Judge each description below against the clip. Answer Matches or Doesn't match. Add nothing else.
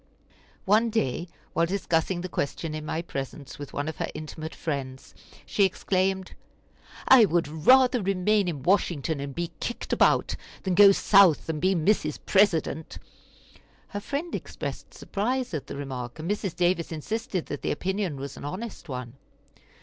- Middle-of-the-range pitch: Matches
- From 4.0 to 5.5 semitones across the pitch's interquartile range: Matches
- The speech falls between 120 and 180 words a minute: Matches